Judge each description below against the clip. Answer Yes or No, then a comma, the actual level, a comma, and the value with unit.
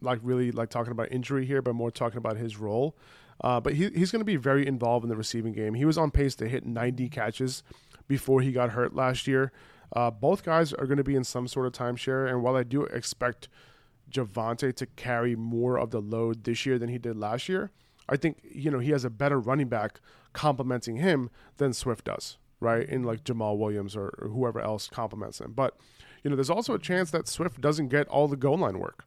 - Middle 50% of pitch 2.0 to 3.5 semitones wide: Yes, average, 3.0 semitones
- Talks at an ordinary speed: No, fast, 235 wpm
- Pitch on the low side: Yes, low, 125 Hz